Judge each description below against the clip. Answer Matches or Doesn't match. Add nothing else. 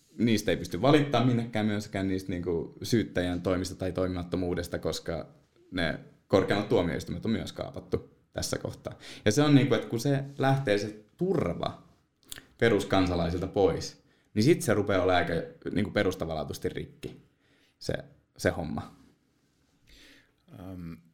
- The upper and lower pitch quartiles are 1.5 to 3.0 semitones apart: Doesn't match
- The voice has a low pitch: Matches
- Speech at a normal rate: Matches